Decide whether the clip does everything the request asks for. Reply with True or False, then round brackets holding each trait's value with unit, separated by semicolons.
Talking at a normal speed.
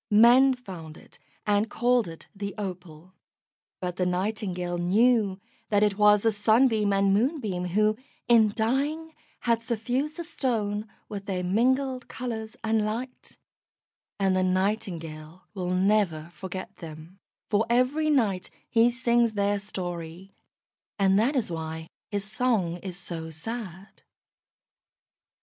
False (130 wpm)